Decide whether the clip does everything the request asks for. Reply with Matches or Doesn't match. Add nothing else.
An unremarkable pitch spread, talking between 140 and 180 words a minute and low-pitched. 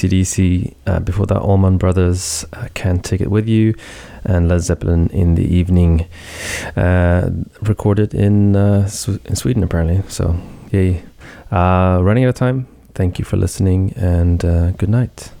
Matches